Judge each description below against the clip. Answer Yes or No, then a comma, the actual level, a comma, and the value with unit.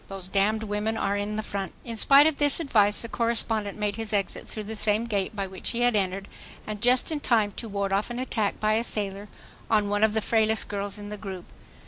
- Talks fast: Yes, fast, 240 wpm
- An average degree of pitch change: No, narrow, 1.9 semitones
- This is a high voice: Yes, high, 210 Hz